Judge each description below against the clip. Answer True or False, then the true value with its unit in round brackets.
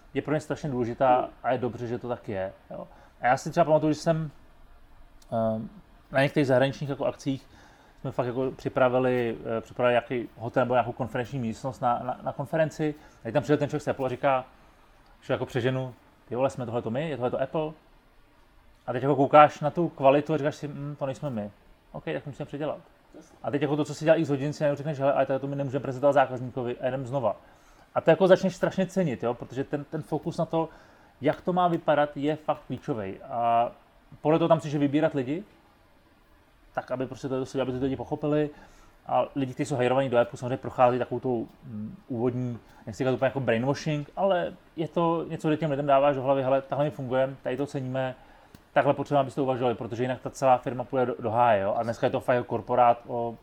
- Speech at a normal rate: False (225 wpm)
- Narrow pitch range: False (3.1 semitones)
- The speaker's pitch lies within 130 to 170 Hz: True (135 Hz)